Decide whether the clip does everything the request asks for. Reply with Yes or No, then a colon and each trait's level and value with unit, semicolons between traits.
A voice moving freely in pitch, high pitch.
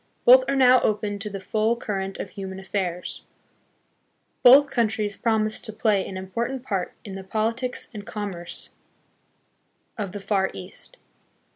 No: average, 3.3 semitones; high, 210 Hz